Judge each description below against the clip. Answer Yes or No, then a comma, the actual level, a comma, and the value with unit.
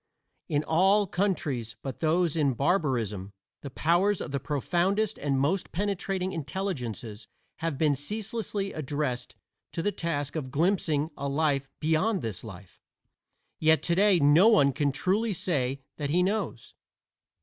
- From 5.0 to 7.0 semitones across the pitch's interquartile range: Yes, wide, 5.5 semitones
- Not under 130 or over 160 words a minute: Yes, average, 140 wpm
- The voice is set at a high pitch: No, medium, 155 Hz